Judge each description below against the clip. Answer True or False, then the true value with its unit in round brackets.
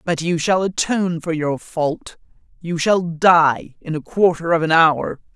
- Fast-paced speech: False (180 wpm)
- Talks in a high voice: False (165 Hz)